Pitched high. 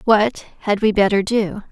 Yes: high, 205 Hz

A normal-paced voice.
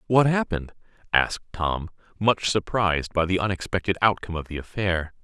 Yes: average, 150 wpm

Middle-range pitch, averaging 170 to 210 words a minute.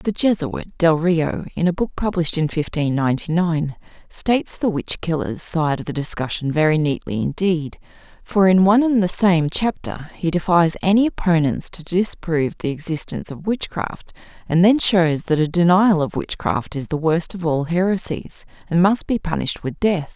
Yes: medium, 170 Hz; average, 175 wpm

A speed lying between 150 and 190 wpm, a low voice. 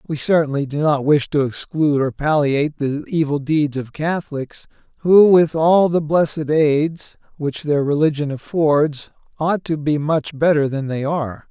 No: average, 165 wpm; medium, 150 Hz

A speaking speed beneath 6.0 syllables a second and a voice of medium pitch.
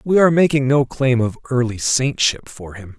No: 5.0 syllables/s; low, 130 Hz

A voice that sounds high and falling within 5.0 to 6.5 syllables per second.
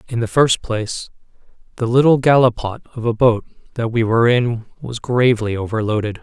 No: low, 115 Hz; 5.4 syllables/s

